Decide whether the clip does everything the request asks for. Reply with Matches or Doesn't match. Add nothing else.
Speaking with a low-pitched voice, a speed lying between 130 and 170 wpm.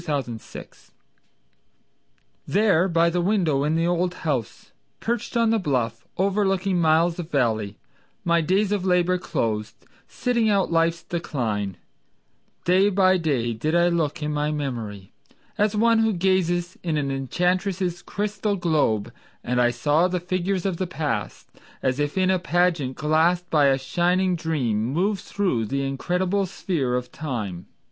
Doesn't match